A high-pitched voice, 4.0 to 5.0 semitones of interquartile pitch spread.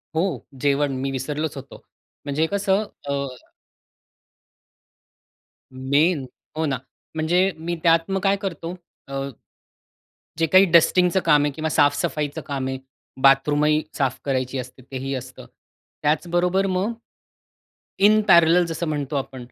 No: medium, 155 Hz; average, 4.3 semitones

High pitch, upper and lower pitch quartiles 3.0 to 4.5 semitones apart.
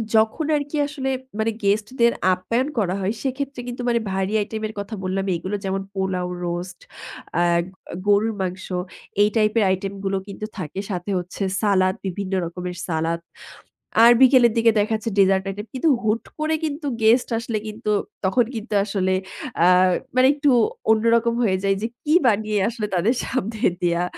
Yes: high, 210 Hz; average, 3.7 semitones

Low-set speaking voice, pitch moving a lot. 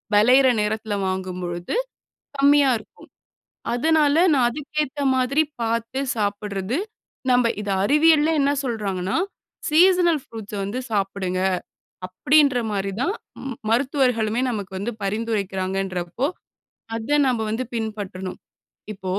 No: high, 225 Hz; wide, 5.9 semitones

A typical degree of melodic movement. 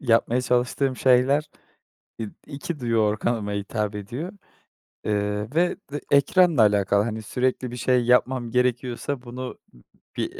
Yes: average, 3.4 semitones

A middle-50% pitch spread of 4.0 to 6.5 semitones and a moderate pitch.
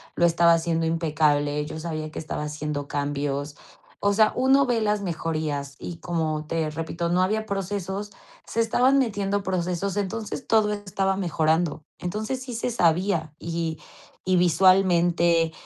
Yes: average, 4.3 semitones; medium, 170 Hz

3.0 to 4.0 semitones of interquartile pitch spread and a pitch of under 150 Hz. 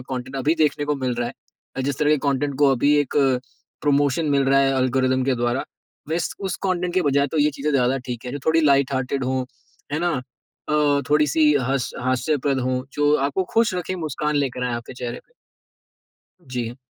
No: narrow, 2.6 semitones; medium, 140 Hz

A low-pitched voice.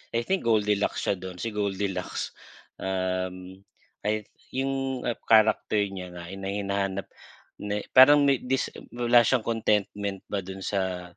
Yes: low, 100 Hz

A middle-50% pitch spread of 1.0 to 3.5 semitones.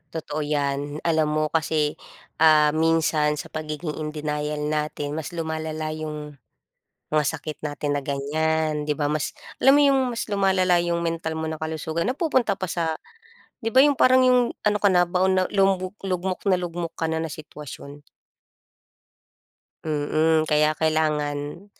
Yes: average, 2.8 semitones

